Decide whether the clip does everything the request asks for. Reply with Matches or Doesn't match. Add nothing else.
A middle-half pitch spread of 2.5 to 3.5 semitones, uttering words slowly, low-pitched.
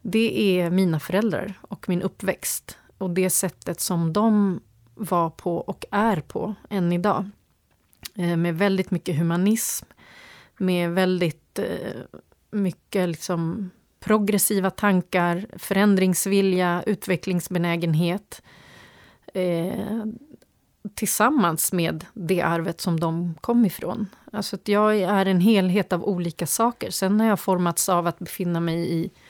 Doesn't match